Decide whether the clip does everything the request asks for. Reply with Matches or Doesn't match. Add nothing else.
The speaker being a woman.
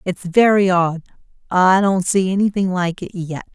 Matches